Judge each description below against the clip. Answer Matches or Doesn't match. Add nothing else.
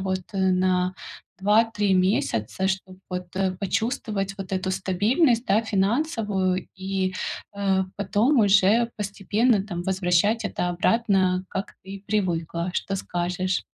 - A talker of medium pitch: Doesn't match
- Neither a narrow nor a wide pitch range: Doesn't match